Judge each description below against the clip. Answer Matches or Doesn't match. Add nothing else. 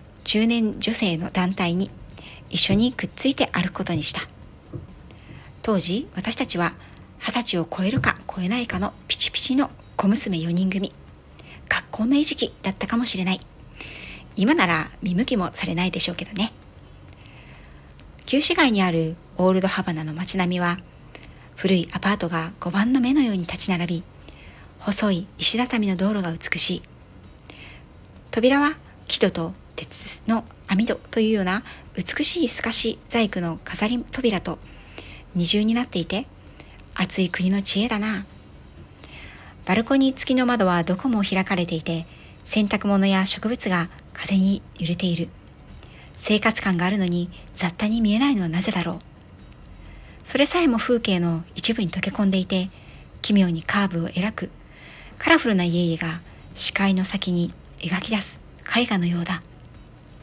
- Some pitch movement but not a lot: Matches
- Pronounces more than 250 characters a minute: Matches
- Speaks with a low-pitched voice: Doesn't match